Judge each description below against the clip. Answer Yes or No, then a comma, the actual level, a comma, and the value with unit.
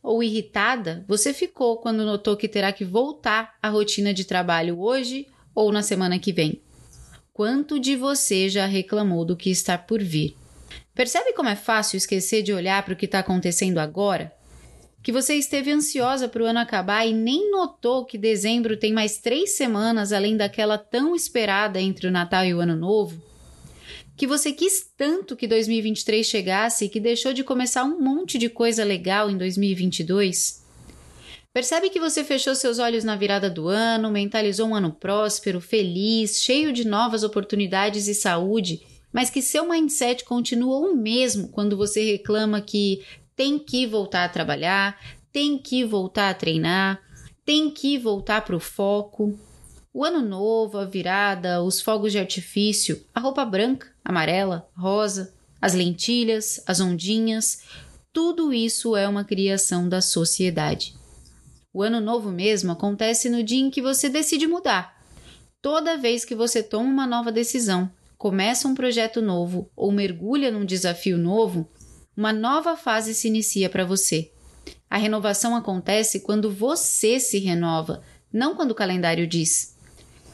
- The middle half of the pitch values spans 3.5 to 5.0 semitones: Yes, average, 4.1 semitones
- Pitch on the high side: Yes, high, 215 Hz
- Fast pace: No, average, 160 wpm